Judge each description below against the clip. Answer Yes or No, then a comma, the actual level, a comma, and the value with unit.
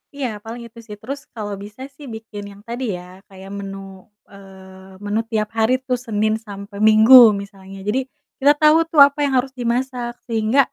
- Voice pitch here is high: Yes, high, 220 Hz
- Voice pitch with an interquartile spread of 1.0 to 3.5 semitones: No, average, 3.9 semitones